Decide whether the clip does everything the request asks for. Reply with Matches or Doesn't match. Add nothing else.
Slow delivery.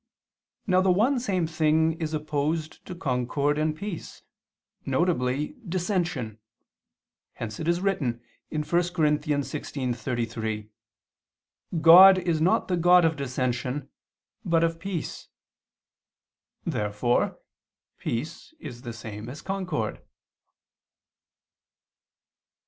Matches